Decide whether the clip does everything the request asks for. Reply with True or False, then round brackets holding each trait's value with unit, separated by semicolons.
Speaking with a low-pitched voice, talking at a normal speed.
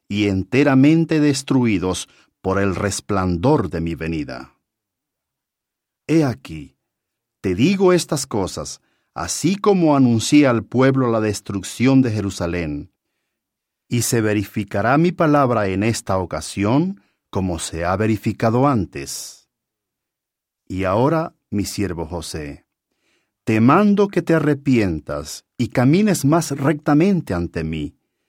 False (115 Hz; 110 wpm)